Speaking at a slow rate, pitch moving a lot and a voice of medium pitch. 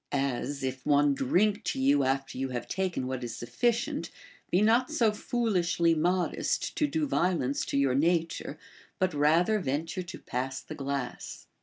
No: average, 165 wpm; wide, 5.7 semitones; medium, 150 Hz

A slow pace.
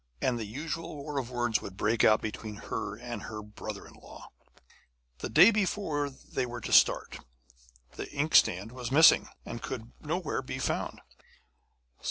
No: average, 160 wpm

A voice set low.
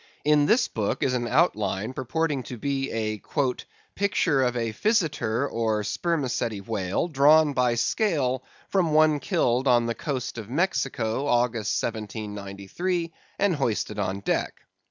Yes: low, 125 Hz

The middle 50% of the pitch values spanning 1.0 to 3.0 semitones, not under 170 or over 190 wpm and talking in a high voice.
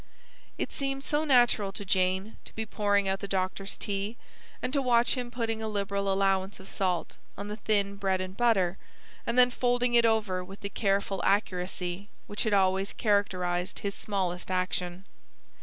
Yes: average, 2.7 semitones; average, 175 wpm; high, 200 Hz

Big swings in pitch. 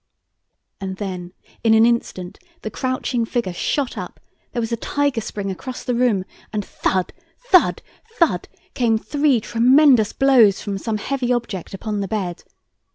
No: average, 4.3 semitones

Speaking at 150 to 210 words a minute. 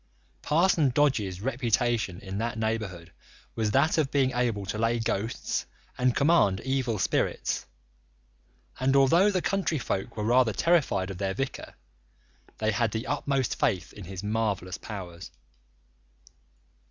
No: slow, 135 wpm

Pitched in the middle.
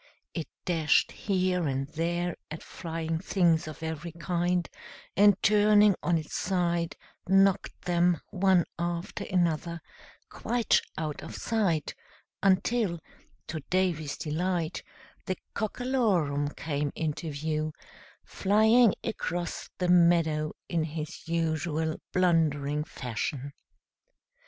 Yes: medium, 170 Hz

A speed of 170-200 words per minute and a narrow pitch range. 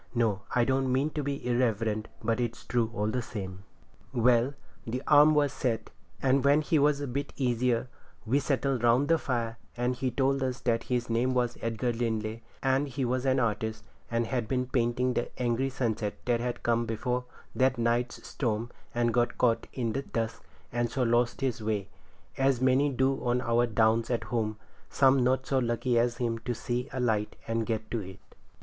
Yes: average, 195 wpm; narrow, 2.2 semitones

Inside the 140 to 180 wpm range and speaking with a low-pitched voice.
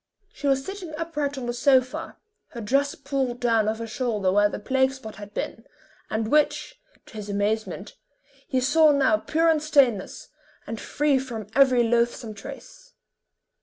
No: average, 165 wpm; very high, 255 Hz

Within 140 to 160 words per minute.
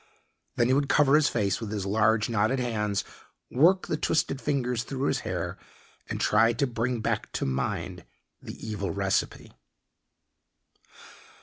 Yes: average, 145 wpm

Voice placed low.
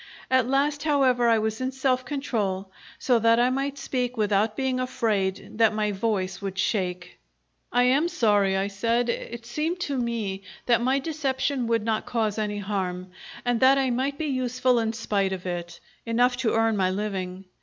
No: high, 230 Hz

